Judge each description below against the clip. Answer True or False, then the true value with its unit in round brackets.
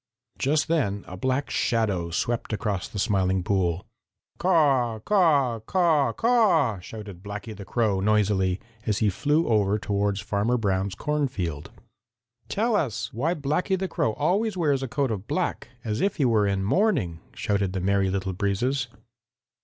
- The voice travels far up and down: True (6.8 semitones)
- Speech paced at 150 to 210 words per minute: True (155 wpm)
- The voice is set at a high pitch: False (110 Hz)